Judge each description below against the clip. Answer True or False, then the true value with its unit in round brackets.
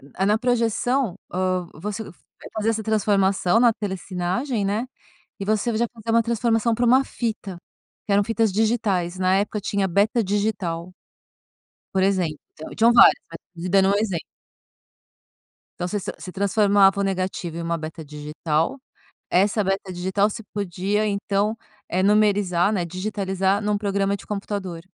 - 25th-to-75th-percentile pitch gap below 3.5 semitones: True (2.8 semitones)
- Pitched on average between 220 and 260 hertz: False (200 Hz)